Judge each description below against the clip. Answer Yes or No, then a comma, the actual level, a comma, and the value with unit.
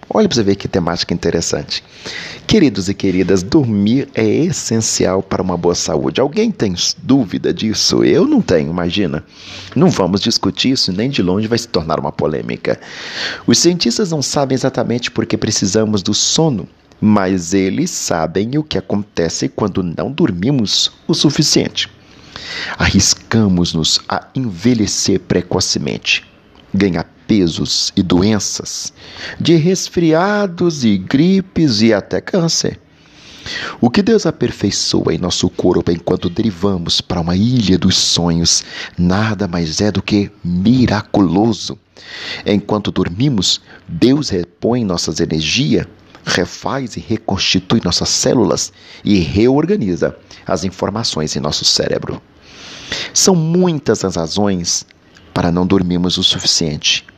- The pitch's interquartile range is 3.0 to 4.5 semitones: No, wide, 5.5 semitones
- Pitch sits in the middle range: No, low, 100 Hz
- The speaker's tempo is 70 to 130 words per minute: Yes, average, 125 wpm